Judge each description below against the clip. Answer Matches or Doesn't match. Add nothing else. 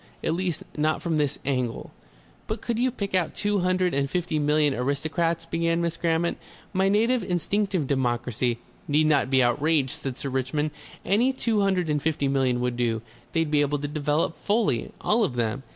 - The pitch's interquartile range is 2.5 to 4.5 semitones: Doesn't match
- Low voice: Doesn't match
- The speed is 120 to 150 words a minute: Doesn't match